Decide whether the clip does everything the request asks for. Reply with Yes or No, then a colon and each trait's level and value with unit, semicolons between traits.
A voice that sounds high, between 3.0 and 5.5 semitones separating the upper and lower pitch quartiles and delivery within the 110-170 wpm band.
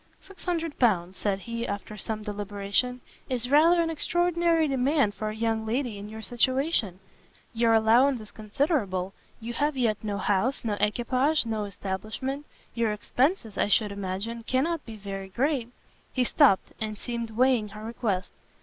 Yes: high, 230 Hz; average, 4.3 semitones; average, 160 wpm